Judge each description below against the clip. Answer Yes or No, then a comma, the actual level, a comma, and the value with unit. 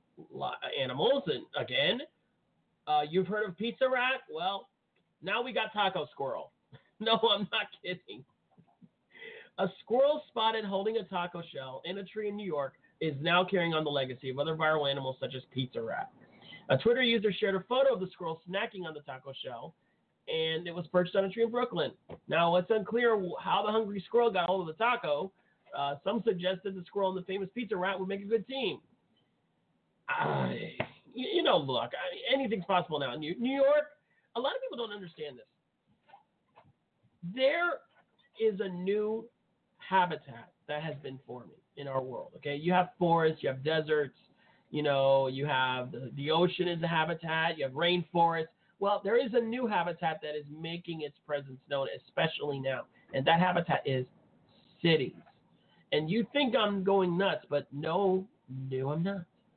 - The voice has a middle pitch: Yes, medium, 180 Hz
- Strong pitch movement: Yes, wide, 6.3 semitones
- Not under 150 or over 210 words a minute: Yes, average, 180 wpm